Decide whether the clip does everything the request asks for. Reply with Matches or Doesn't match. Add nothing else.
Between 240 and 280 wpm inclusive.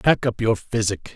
Doesn't match